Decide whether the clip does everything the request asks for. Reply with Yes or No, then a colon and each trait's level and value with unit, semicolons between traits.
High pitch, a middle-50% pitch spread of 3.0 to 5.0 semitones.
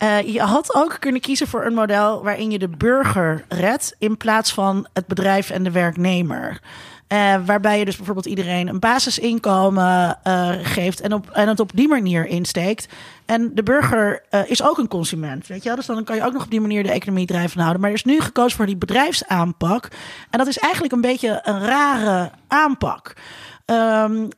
Yes: high, 210 Hz; average, 3.8 semitones